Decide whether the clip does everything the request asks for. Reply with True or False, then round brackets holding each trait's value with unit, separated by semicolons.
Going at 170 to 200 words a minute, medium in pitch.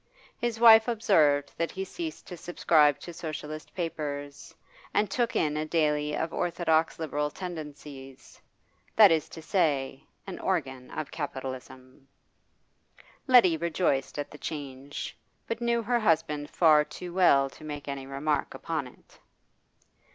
False (135 wpm; 155 Hz)